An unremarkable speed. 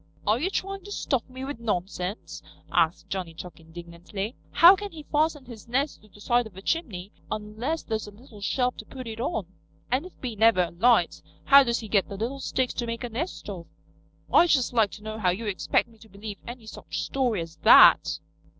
No: fast, 215 wpm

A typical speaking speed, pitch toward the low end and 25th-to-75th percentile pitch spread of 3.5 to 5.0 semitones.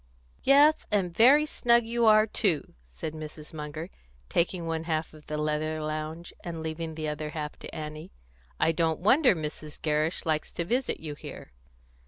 No: average, 170 wpm; medium, 160 Hz; average, 4.2 semitones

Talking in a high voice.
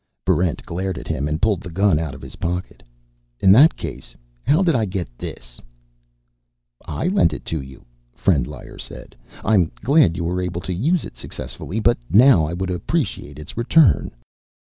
No: very low, 90 Hz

